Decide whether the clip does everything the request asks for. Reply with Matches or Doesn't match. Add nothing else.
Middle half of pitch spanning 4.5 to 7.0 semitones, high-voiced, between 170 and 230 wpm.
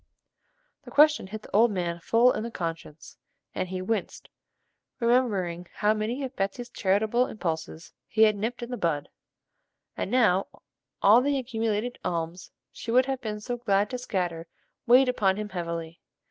Doesn't match